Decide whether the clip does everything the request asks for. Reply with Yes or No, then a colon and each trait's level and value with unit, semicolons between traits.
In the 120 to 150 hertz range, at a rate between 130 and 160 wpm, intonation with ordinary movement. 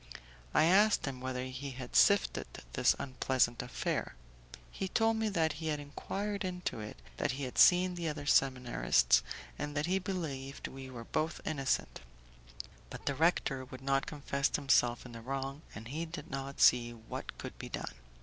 No: medium, 140 Hz; average, 175 wpm; average, 4.3 semitones